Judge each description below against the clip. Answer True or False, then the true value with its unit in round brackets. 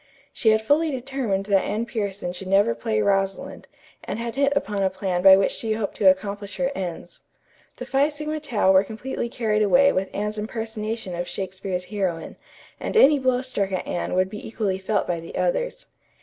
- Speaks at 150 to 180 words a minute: False (190 wpm)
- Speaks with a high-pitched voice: True (210 Hz)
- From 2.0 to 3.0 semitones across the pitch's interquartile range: False (4.5 semitones)